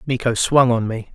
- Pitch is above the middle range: No, low, 120 Hz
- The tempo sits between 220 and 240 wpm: No, fast, 210 wpm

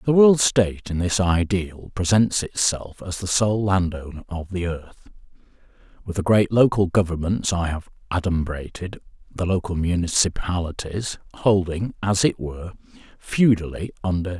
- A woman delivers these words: No, male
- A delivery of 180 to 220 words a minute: No, average, 145 wpm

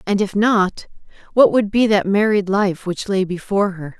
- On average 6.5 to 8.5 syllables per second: No, 4.8 syllables/s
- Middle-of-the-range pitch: No, high, 200 Hz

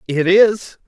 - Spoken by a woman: No, male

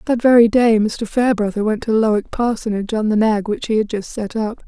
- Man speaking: No, female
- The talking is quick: Yes, fast, 230 wpm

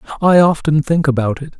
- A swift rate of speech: No, average, 190 wpm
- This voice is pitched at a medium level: Yes, medium, 150 Hz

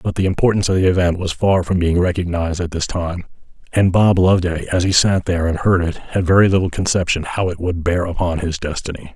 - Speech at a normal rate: No, fast, 230 wpm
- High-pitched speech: No, very low, 90 Hz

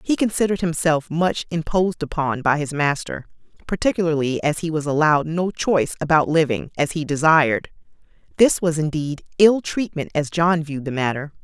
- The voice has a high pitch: No, medium, 160 Hz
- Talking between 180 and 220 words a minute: No, average, 165 wpm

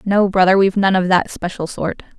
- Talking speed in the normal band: No, fast, 220 wpm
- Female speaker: Yes, female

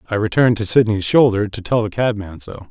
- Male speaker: Yes, male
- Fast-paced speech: Yes, fast, 220 wpm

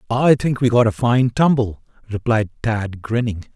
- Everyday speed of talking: Yes, average, 170 wpm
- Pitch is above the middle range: No, low, 115 Hz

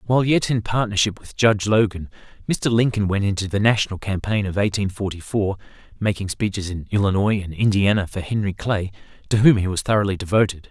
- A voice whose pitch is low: Yes, low, 100 Hz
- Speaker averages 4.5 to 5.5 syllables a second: No, 6.0 syllables/s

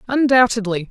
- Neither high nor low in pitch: No, high, 225 Hz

